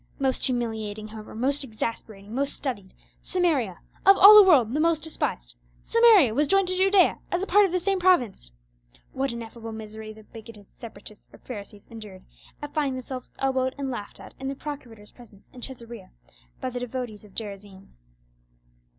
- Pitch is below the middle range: No, high, 245 Hz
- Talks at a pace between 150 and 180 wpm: Yes, average, 165 wpm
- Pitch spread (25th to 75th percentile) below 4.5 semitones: No, wide, 5.4 semitones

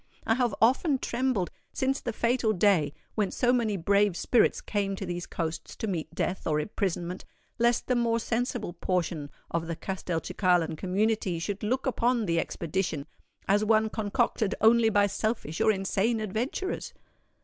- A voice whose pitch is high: Yes, high, 205 Hz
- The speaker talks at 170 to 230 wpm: No, average, 155 wpm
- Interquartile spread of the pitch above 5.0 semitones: No, average, 4.6 semitones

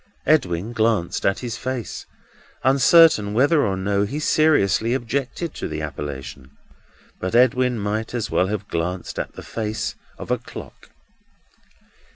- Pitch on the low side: Yes, low, 110 Hz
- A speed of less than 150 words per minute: Yes, average, 140 wpm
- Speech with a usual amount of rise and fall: Yes, average, 4.9 semitones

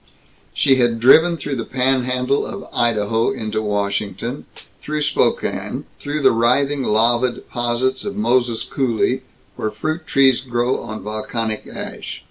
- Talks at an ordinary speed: No, slow, 130 wpm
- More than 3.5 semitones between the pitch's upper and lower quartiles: No, average, 3.1 semitones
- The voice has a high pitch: No, low, 125 Hz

